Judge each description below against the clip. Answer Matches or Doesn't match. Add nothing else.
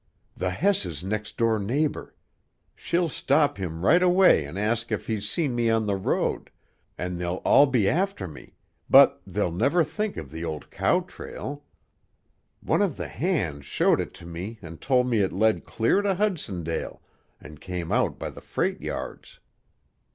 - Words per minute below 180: Matches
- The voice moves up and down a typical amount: Doesn't match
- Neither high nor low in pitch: Doesn't match